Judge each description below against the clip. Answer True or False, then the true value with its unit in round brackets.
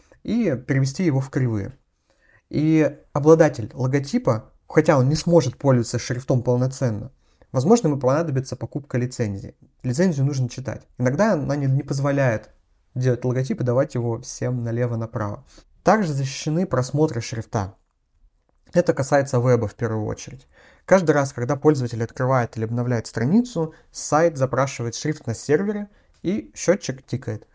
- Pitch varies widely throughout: False (3.9 semitones)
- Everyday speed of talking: True (130 wpm)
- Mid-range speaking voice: False (130 Hz)